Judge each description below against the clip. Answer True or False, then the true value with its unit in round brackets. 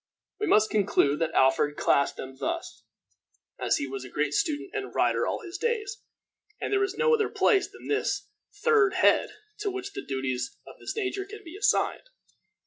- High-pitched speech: True (375 Hz)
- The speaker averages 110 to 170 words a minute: False (185 wpm)